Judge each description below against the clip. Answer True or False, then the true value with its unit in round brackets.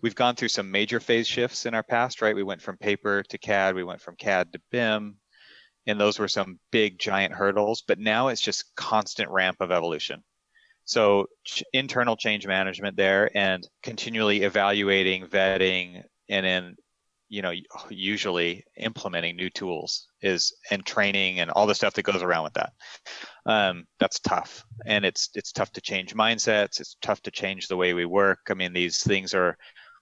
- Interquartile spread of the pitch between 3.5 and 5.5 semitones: False (2.7 semitones)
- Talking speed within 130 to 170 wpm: False (180 wpm)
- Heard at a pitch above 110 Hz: False (100 Hz)